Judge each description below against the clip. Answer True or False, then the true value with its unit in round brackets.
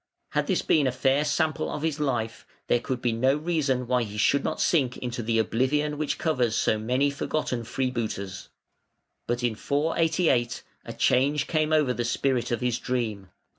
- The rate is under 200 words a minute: True (175 wpm)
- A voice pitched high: False (125 Hz)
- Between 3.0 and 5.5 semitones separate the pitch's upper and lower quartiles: True (3.8 semitones)